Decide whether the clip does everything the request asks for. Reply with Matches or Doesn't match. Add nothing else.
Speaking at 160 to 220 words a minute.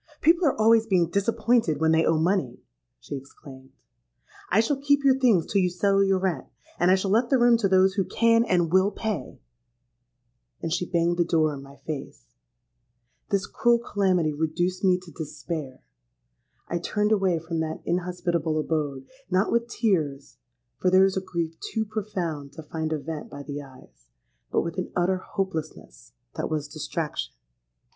Matches